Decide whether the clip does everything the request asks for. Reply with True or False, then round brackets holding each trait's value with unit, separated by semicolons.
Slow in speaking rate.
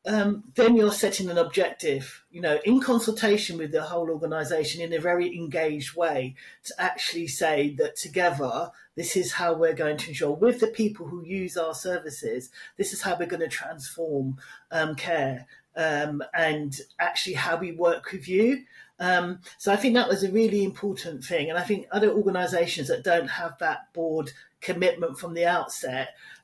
False (180 wpm)